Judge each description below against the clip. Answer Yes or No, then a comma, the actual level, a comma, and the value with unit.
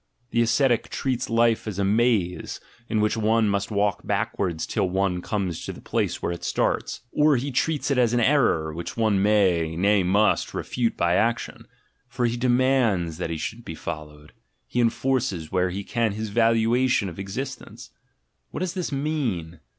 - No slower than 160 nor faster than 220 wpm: Yes, average, 180 wpm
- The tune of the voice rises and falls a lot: No, average, 5.0 semitones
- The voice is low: Yes, low, 110 Hz